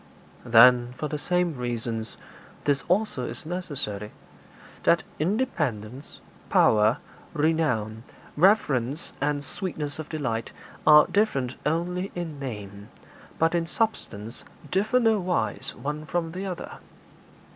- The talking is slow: Yes, slow, 115 wpm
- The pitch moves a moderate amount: No, wide, 6.6 semitones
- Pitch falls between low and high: Yes, medium, 150 Hz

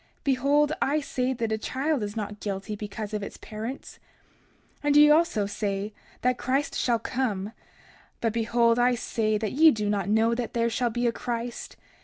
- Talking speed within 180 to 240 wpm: Yes, average, 185 wpm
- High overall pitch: Yes, high, 230 Hz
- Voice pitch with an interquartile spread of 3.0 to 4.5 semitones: Yes, average, 3.4 semitones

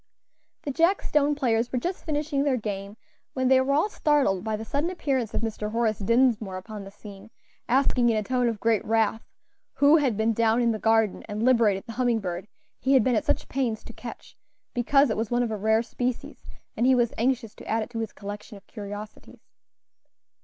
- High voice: Yes, high, 230 Hz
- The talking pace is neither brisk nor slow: No, fast, 210 wpm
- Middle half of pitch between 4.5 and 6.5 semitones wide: No, average, 3.4 semitones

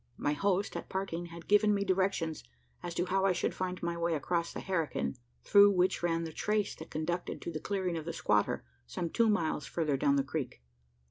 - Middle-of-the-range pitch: Yes, medium, 170 Hz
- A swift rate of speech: Yes, fast, 210 wpm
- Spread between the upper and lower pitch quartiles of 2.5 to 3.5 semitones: Yes, average, 3.1 semitones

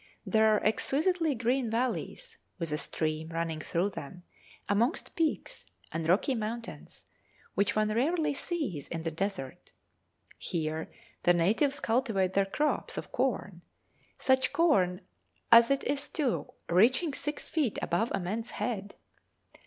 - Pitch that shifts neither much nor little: No, wide, 7.2 semitones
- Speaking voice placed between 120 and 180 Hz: No, high, 220 Hz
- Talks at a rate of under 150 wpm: Yes, slow, 135 wpm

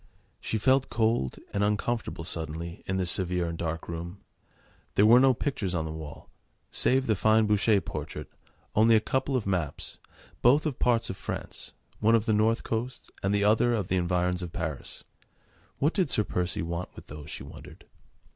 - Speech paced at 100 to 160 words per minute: No, average, 185 wpm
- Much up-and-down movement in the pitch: No, average, 5.0 semitones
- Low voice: Yes, low, 100 Hz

